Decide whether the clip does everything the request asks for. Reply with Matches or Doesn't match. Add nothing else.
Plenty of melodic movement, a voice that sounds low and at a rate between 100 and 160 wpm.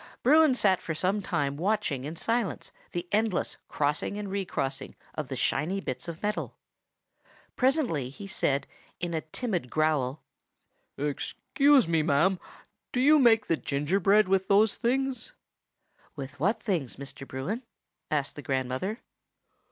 Doesn't match